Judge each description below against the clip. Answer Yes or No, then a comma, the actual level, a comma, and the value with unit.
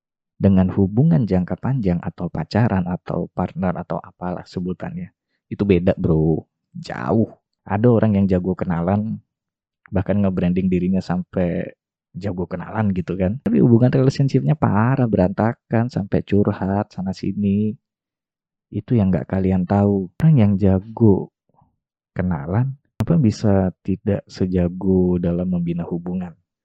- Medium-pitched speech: No, very low, 95 Hz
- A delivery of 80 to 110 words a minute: No, average, 120 wpm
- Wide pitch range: No, average, 3.2 semitones